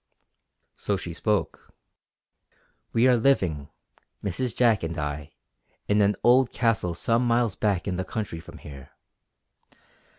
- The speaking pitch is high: No, low, 105 Hz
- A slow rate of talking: Yes, slow, 130 wpm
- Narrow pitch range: No, wide, 5.6 semitones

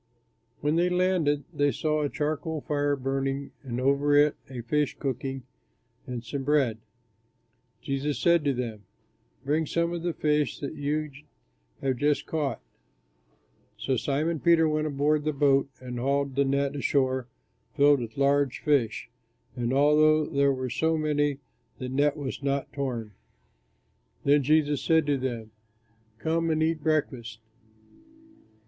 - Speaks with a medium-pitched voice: Yes, medium, 145 Hz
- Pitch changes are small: Yes, narrow, 2.3 semitones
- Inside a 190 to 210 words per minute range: No, average, 140 wpm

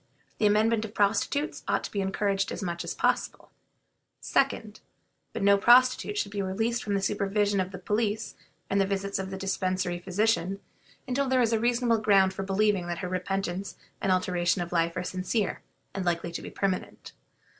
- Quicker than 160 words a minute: Yes, average, 180 wpm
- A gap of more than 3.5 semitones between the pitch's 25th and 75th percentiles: No, narrow, 2.5 semitones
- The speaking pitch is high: Yes, high, 195 Hz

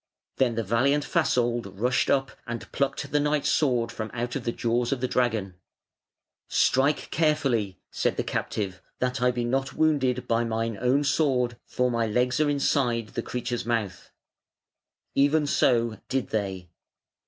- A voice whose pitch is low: Yes, low, 125 Hz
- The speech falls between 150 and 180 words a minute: Yes, average, 155 wpm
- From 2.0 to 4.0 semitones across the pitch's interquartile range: Yes, average, 2.9 semitones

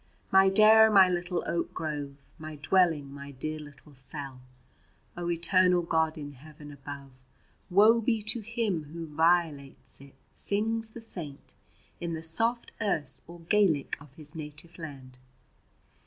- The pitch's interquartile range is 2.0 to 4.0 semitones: No, average, 4.8 semitones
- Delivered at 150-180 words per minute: No, average, 140 wpm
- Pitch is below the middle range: No, medium, 160 Hz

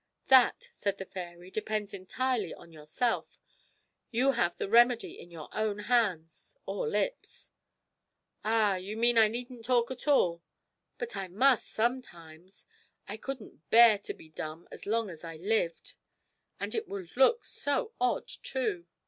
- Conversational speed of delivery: Yes, average, 150 wpm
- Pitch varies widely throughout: Yes, wide, 5.7 semitones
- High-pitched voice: Yes, high, 215 Hz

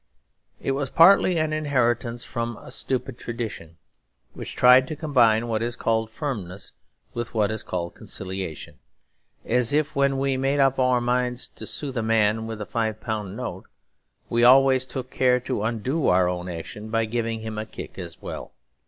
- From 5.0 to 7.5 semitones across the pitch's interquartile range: No, average, 3.3 semitones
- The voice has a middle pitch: No, low, 120 Hz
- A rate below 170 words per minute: No, average, 175 wpm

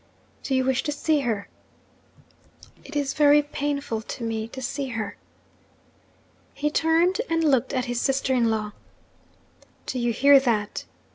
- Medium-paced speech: Yes, average, 150 wpm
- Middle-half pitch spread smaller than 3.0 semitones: No, average, 3.7 semitones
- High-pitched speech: Yes, very high, 265 Hz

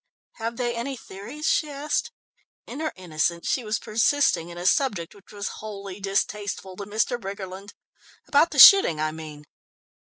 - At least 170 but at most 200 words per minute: No, average, 160 wpm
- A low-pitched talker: No, high, 205 Hz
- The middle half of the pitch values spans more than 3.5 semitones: Yes, average, 4.8 semitones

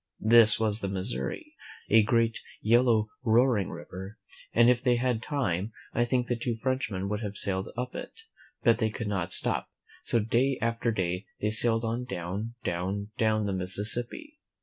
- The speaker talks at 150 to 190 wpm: Yes, average, 170 wpm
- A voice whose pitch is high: No, low, 115 Hz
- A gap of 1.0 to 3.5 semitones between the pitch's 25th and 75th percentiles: Yes, average, 3.0 semitones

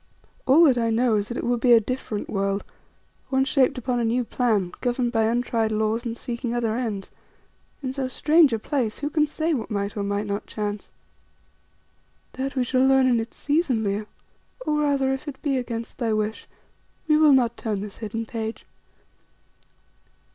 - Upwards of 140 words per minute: Yes, average, 185 wpm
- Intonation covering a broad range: No, average, 3.3 semitones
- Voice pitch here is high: Yes, high, 240 Hz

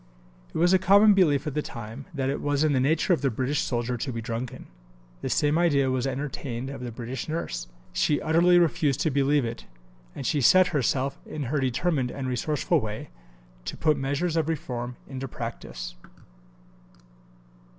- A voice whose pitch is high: No, medium, 140 Hz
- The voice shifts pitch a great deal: No, average, 3.8 semitones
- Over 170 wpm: Yes, average, 180 wpm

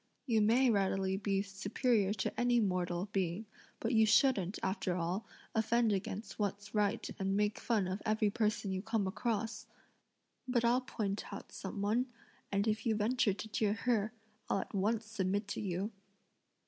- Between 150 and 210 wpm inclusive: Yes, average, 165 wpm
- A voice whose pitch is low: No, high, 210 Hz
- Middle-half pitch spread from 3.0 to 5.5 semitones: No, narrow, 2.5 semitones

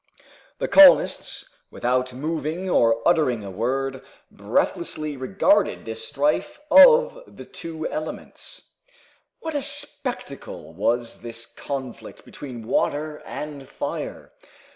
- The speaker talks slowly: Yes, slow, 105 wpm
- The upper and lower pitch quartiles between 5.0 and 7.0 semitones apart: Yes, wide, 5.6 semitones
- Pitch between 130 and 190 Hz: Yes, medium, 140 Hz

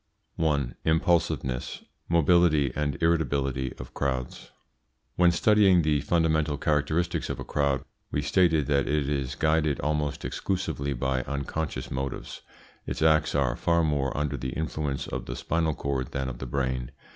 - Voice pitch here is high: No, very low, 75 Hz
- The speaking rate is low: No, average, 145 wpm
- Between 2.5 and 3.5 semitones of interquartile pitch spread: Yes, average, 2.9 semitones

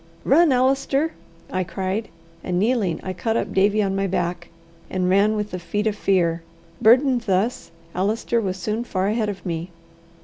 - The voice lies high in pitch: Yes, high, 200 Hz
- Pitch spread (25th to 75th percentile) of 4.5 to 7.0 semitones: No, average, 3.6 semitones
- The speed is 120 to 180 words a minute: Yes, average, 170 wpm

